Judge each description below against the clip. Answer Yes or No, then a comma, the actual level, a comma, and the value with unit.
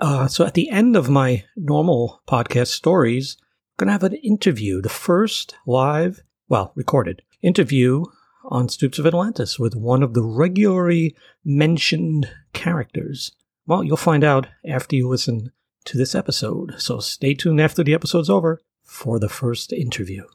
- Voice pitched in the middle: Yes, medium, 150 Hz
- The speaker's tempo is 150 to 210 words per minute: Yes, average, 160 wpm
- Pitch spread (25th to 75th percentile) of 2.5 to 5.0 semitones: No, wide, 5.5 semitones